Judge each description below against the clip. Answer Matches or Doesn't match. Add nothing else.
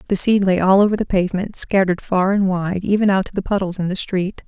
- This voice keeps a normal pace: Doesn't match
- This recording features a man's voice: Doesn't match